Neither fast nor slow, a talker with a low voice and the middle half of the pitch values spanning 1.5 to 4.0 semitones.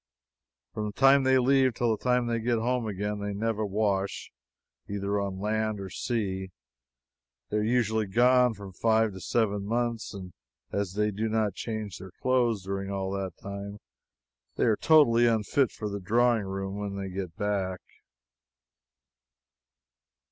Yes: average, 150 wpm; low, 105 Hz; average, 2.9 semitones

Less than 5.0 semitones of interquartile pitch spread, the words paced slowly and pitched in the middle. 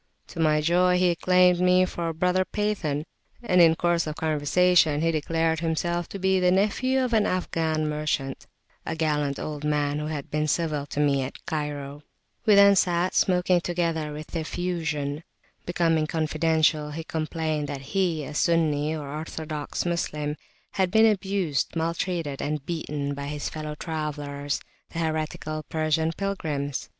No: average, 2.9 semitones; average, 155 wpm; medium, 160 Hz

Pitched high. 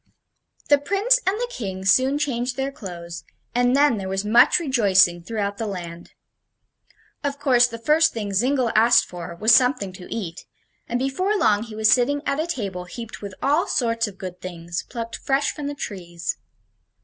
Yes: high, 230 Hz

